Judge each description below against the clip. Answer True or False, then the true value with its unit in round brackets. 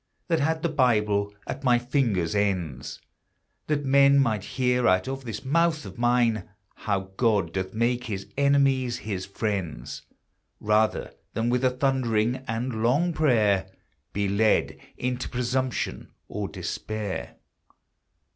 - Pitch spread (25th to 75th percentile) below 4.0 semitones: False (4.4 semitones)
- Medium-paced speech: False (130 wpm)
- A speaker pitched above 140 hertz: False (120 Hz)